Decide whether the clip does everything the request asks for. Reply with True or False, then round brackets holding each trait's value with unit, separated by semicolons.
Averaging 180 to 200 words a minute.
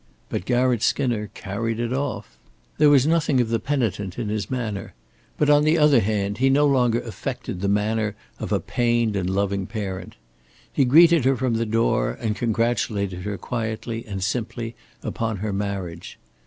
False (170 wpm)